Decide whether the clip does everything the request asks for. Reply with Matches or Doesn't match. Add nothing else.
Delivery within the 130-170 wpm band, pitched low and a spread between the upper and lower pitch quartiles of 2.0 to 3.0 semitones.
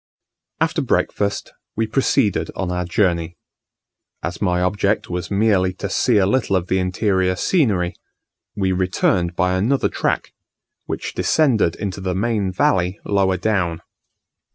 Matches